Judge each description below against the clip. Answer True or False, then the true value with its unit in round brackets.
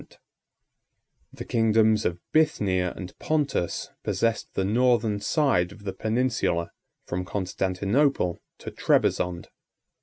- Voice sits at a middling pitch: False (105 Hz)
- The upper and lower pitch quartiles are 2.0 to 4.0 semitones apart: False (4.8 semitones)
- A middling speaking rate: False (100 wpm)